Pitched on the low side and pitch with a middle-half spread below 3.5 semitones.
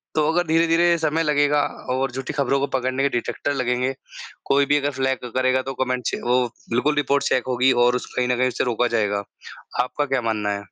Yes: low, 130 Hz; narrow, 2.6 semitones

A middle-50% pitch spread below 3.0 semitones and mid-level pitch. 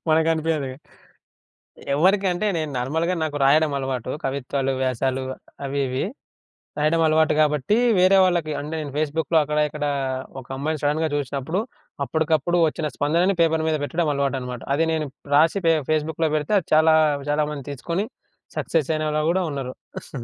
Yes: narrow, 2.5 semitones; medium, 155 Hz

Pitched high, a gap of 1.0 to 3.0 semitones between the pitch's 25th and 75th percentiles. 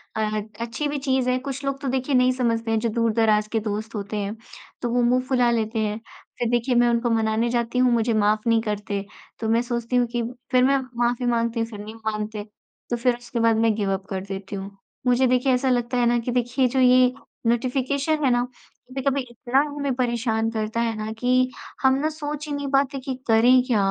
Yes: high, 240 Hz; narrow, 2.4 semitones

